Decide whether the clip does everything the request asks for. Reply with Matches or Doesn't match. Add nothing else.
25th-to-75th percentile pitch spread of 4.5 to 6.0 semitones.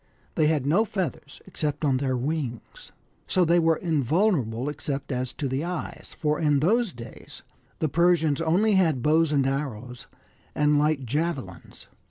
Doesn't match